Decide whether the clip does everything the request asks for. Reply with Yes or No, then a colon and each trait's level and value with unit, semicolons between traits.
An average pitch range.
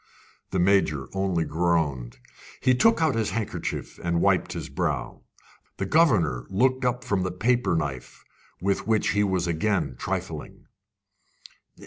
No: wide, 5.7 semitones